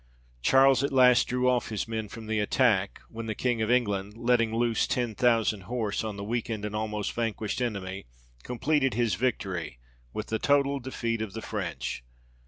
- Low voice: Yes, low, 115 Hz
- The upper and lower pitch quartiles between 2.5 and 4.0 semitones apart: Yes, average, 2.9 semitones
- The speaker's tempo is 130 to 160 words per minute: No, average, 180 wpm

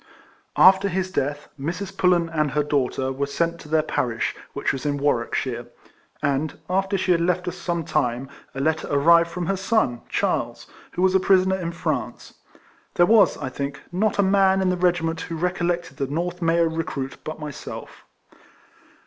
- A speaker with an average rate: Yes, average, 185 wpm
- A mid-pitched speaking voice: Yes, medium, 170 Hz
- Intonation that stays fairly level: No, average, 4.2 semitones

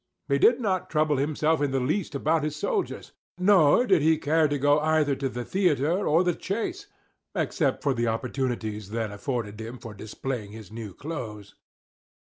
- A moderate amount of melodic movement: No, wide, 5.7 semitones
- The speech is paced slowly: No, average, 175 wpm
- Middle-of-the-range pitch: Yes, medium, 145 Hz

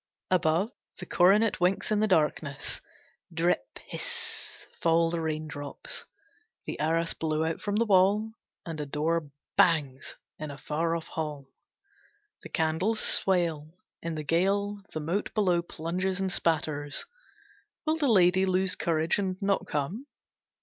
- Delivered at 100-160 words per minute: Yes, average, 140 wpm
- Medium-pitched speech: Yes, medium, 170 Hz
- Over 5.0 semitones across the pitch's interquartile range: No, average, 3.5 semitones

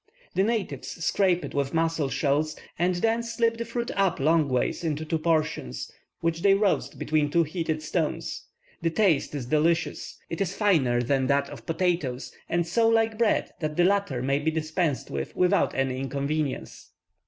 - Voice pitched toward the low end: No, medium, 160 Hz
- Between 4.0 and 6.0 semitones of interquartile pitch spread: Yes, average, 4.8 semitones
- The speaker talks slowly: No, average, 175 wpm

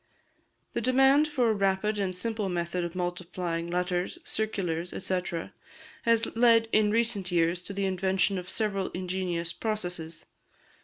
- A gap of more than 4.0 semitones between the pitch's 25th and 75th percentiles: No, average, 3.6 semitones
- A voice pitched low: No, high, 190 Hz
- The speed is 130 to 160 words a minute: Yes, average, 140 wpm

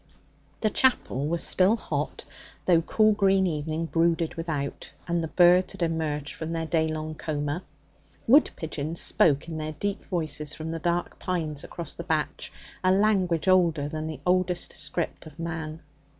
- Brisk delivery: No, average, 165 wpm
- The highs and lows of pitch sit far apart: No, narrow, 2.4 semitones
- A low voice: No, medium, 165 Hz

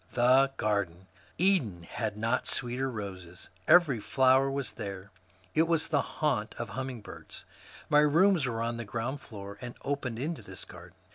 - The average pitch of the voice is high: No, low, 120 Hz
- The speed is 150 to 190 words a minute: Yes, average, 155 wpm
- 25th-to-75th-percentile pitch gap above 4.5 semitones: Yes, average, 5.2 semitones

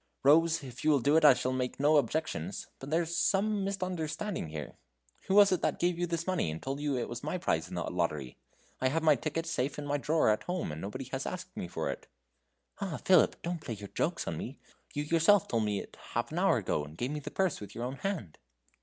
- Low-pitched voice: No, medium, 150 Hz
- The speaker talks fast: Yes, fast, 245 wpm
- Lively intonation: Yes, wide, 5.9 semitones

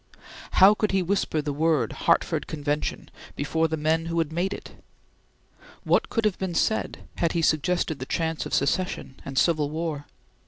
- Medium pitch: Yes, medium, 160 Hz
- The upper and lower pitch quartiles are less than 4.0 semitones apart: Yes, average, 3.2 semitones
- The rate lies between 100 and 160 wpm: No, average, 170 wpm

